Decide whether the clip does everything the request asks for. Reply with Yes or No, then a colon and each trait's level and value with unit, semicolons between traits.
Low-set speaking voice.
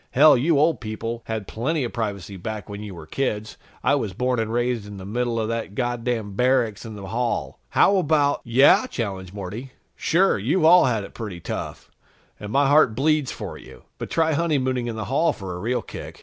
Yes: low, 120 Hz